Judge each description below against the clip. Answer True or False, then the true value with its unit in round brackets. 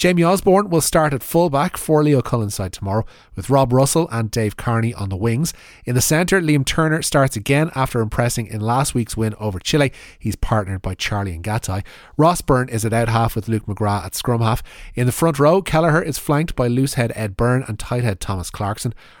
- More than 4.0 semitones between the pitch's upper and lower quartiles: True (5.5 semitones)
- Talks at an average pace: False (215 wpm)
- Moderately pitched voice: False (120 Hz)